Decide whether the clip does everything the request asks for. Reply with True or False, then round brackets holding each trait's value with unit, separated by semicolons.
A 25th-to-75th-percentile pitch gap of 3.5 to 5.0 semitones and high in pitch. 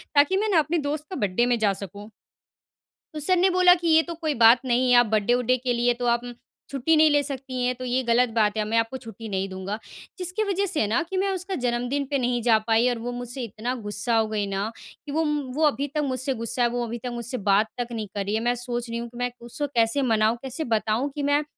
True (4.2 semitones; 245 Hz)